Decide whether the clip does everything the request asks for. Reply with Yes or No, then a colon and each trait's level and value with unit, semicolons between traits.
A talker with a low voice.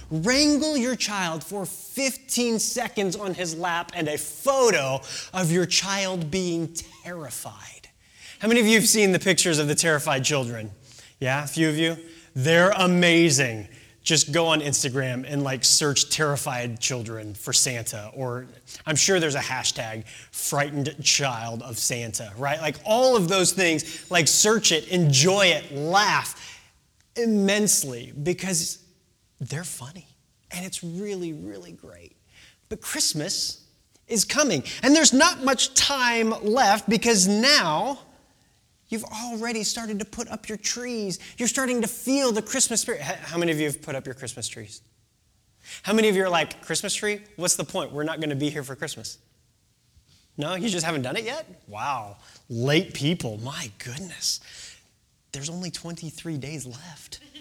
No: medium, 165 Hz